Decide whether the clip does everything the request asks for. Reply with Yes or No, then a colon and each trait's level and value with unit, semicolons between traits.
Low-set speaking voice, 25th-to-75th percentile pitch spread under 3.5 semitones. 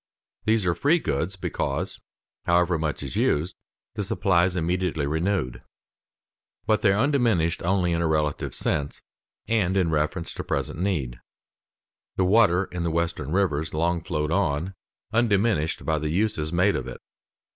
No: very low, 85 Hz; average, 3.8 semitones